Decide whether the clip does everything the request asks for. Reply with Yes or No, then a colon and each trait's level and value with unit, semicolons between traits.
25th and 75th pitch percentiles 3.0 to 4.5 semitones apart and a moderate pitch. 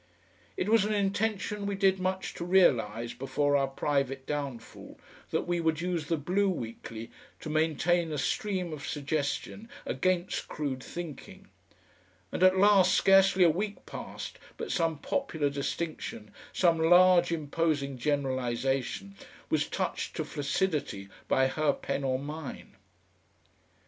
No: average, 5.1 semitones; medium, 160 Hz